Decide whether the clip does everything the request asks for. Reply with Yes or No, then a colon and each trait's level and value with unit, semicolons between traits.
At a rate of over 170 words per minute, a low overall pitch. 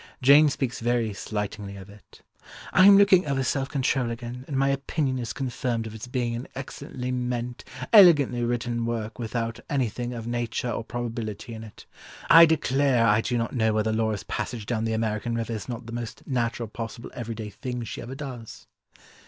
Yes: average, 185 wpm; low, 120 Hz